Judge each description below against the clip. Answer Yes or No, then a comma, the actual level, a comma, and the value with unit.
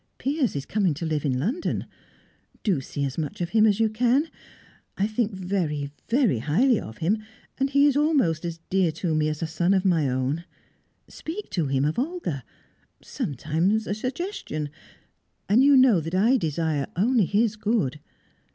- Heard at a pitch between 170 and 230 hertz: Yes, high, 190 Hz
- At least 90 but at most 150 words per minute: No, average, 175 wpm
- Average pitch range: No, wide, 7.5 semitones